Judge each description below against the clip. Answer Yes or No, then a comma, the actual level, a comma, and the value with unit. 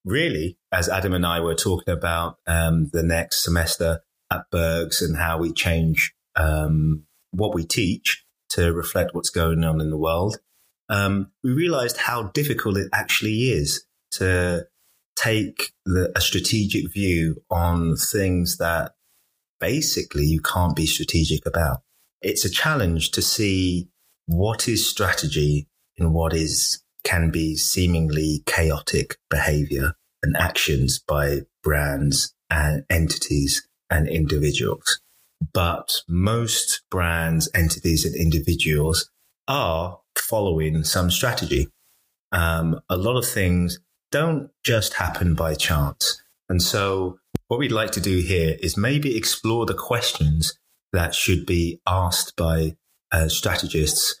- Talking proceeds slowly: Yes, slow, 130 wpm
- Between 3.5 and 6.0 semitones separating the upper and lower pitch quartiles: No, average, 2.7 semitones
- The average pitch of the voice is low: Yes, very low, 85 Hz